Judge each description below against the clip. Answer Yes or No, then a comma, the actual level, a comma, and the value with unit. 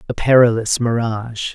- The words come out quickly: No, slow, 115 wpm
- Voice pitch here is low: Yes, low, 115 Hz